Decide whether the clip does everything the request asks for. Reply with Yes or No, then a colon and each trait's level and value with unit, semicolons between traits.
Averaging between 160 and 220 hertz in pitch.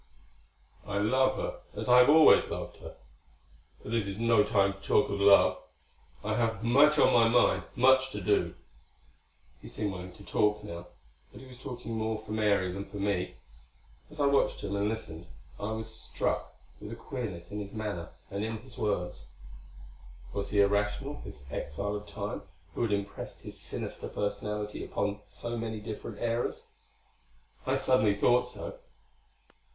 No: low, 105 Hz